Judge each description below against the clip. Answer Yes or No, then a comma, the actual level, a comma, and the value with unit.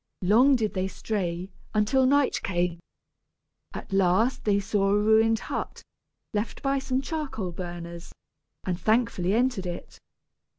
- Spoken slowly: Yes, slow, 130 wpm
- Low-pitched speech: No, high, 210 Hz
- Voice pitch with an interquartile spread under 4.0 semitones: No, average, 5.3 semitones